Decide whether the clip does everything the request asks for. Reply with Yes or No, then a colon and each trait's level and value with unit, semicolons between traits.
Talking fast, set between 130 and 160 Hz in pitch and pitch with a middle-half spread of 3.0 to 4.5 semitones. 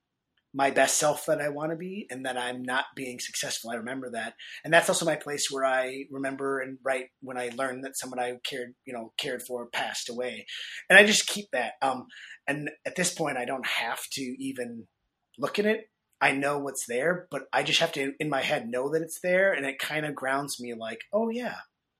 Yes: fast, 225 wpm; low, 135 Hz; average, 3.6 semitones